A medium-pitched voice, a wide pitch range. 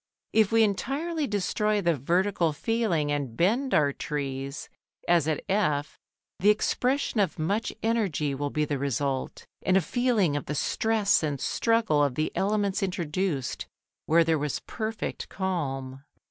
Yes: medium, 175 Hz; wide, 6.5 semitones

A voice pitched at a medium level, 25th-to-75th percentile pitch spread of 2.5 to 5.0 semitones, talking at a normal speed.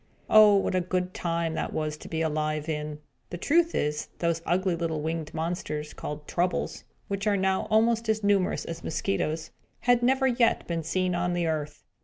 Yes: medium, 175 Hz; average, 4.1 semitones; average, 185 wpm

